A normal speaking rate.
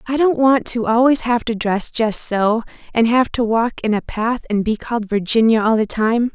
No: fast, 225 wpm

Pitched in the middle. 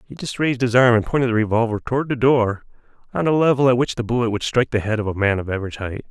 No: low, 120 Hz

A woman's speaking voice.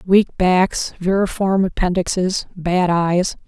Yes: female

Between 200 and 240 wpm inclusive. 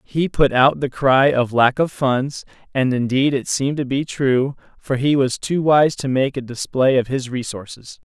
Yes: fast, 205 wpm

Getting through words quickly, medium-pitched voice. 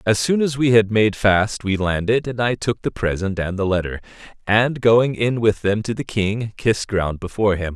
No: fast, 225 wpm; low, 110 Hz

